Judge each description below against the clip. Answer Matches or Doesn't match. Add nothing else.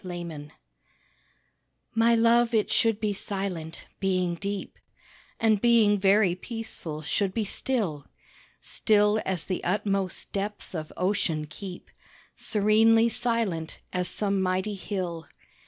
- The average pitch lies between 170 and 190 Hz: Doesn't match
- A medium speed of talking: Doesn't match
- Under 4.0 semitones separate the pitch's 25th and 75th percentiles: Matches